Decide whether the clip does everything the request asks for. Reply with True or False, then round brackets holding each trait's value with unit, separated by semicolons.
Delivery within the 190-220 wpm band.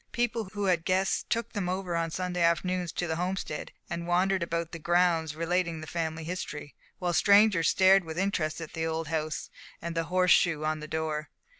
True (200 wpm)